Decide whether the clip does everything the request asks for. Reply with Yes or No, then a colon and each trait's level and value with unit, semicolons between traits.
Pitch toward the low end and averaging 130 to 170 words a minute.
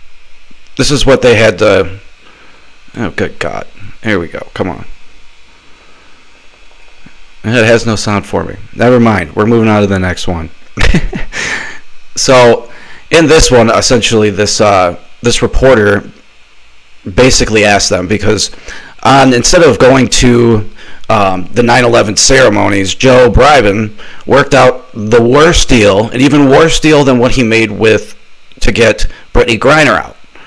Yes: low, 110 Hz; average, 140 wpm